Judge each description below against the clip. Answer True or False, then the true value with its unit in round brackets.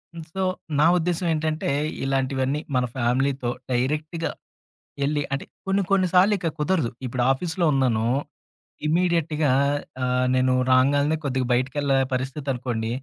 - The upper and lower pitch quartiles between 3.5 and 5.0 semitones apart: True (3.9 semitones)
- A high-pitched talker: False (140 Hz)